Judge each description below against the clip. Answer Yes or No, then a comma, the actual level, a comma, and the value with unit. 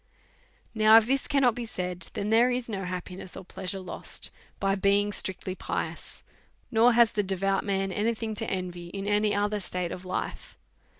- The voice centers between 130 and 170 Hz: No, high, 200 Hz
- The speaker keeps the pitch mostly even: No, average, 3.0 semitones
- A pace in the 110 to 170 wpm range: No, average, 185 wpm